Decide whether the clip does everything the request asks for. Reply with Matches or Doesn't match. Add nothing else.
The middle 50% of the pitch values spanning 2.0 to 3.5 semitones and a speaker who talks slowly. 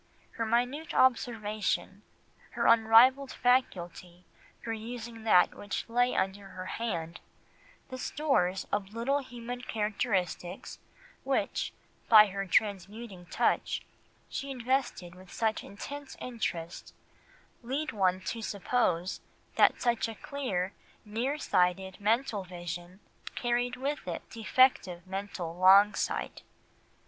Doesn't match